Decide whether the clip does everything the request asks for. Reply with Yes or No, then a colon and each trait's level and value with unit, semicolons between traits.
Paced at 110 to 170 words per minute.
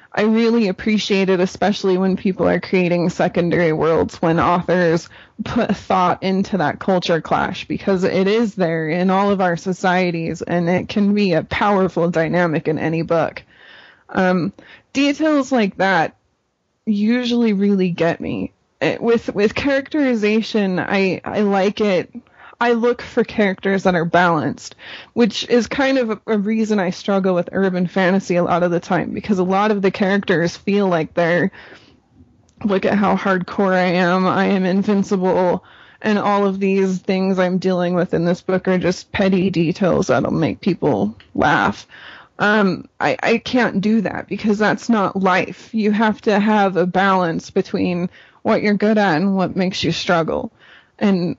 Yes: average, 165 wpm